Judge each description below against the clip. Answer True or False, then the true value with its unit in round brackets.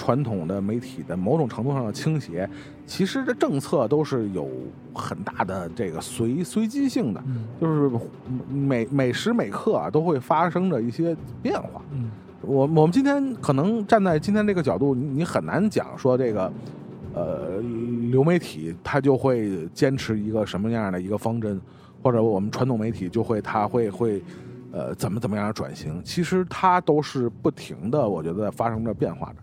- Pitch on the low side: True (130 Hz)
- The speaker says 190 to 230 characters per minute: False (265 characters per minute)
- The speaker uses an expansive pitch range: True (6.0 semitones)